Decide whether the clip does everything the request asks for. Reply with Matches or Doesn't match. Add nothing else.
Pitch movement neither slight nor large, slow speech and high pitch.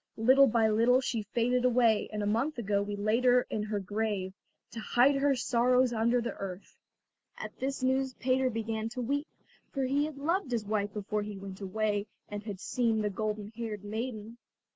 Doesn't match